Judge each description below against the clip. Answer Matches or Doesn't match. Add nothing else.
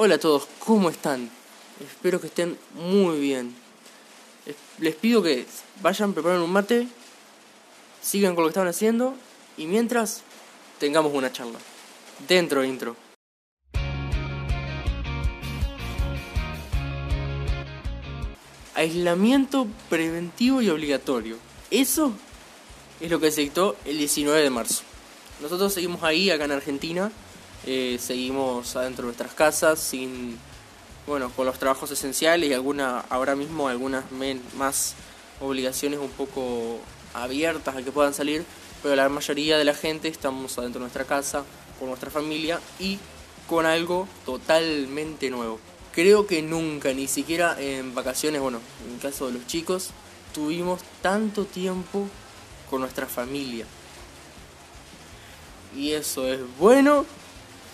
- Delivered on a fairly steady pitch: Doesn't match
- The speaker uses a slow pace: Matches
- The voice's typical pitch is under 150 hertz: Matches